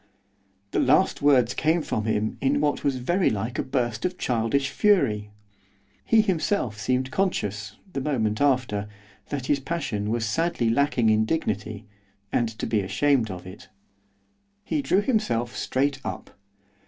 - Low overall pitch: Yes, low, 125 Hz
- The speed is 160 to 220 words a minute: No, average, 150 wpm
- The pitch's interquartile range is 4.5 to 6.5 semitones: Yes, average, 5.2 semitones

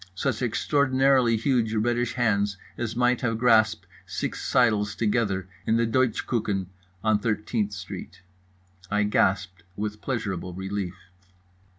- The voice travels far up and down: No, average, 2.9 semitones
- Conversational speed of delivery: No, slow, 120 wpm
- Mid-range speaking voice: No, low, 110 Hz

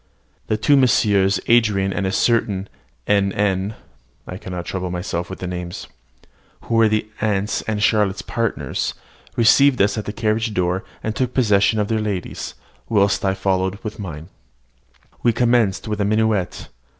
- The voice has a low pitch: Yes, low, 105 Hz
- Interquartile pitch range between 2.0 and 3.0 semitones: Yes, narrow, 2.6 semitones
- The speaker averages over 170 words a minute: No, average, 160 wpm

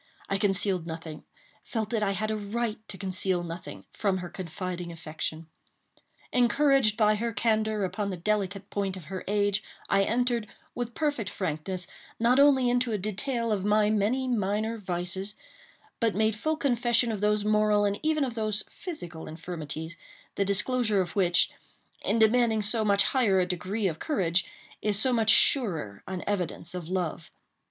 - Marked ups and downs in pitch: No, average, 3.7 semitones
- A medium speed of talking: Yes, average, 160 wpm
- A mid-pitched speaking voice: No, high, 205 Hz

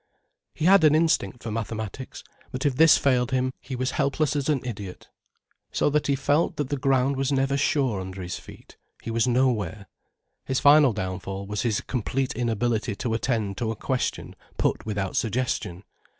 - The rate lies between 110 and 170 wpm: No, average, 180 wpm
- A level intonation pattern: No, average, 4.3 semitones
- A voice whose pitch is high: No, low, 125 Hz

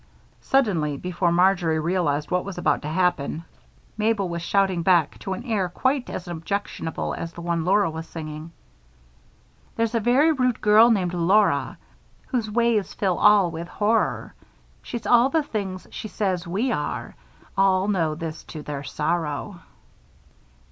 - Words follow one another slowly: No, average, 150 wpm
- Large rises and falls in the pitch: No, average, 4.3 semitones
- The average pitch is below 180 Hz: No, medium, 185 Hz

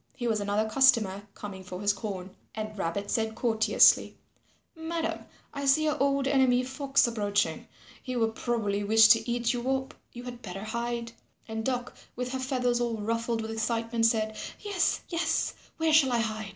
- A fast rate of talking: No, average, 175 wpm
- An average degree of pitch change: Yes, average, 3.2 semitones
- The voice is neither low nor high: No, high, 235 Hz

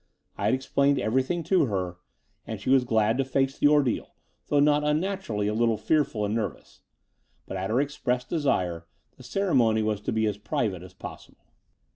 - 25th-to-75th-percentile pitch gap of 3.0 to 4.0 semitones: No, wide, 5.4 semitones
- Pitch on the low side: Yes, low, 120 Hz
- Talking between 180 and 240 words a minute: Yes, average, 185 wpm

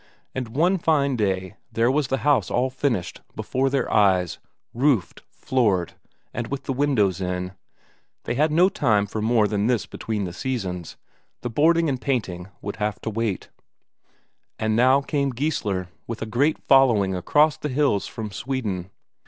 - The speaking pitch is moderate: No, low, 120 Hz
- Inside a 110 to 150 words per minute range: No, average, 160 wpm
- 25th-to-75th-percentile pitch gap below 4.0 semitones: No, average, 5.2 semitones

